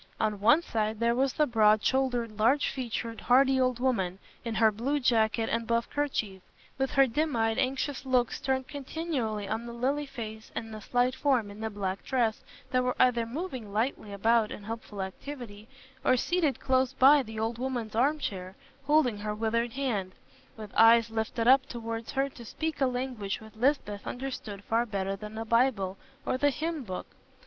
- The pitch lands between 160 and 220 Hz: No, high, 235 Hz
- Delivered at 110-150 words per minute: No, average, 185 wpm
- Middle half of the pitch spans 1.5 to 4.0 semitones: Yes, average, 3.4 semitones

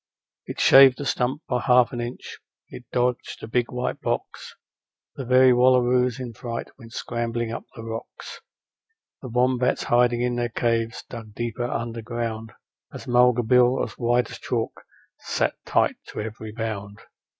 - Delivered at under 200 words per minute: Yes, average, 155 wpm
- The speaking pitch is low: Yes, low, 120 Hz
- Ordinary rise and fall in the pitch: No, narrow, 1.4 semitones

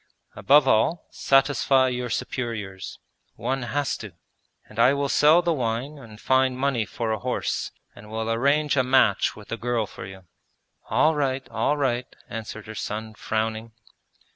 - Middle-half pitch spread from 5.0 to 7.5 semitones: No, average, 3.7 semitones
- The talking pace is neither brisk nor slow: Yes, average, 160 wpm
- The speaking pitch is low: Yes, low, 125 Hz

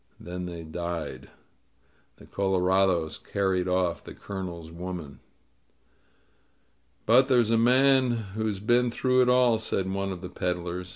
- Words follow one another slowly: Yes, slow, 130 wpm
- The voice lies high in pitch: No, very low, 95 Hz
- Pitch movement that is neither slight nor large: Yes, average, 4.6 semitones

